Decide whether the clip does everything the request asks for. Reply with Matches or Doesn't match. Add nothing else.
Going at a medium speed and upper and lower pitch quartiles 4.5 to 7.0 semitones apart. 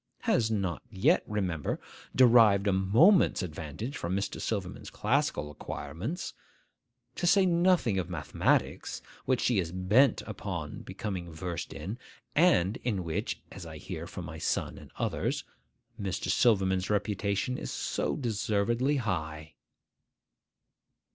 Doesn't match